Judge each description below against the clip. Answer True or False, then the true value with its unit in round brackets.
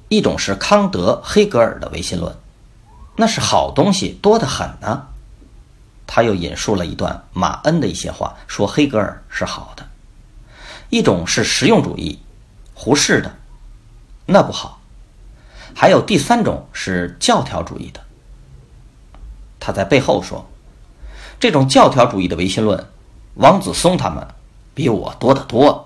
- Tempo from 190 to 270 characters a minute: True (210 characters per minute)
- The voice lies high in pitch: False (120 Hz)